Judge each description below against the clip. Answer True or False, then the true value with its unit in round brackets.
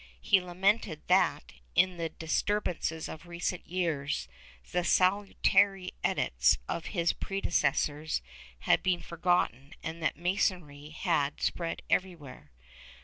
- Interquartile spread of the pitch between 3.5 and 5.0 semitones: False (2.9 semitones)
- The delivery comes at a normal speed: False (115 wpm)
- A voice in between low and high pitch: True (170 Hz)